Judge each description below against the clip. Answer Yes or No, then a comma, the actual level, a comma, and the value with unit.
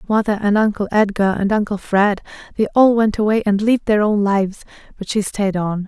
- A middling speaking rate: Yes, average, 195 wpm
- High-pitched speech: Yes, high, 205 Hz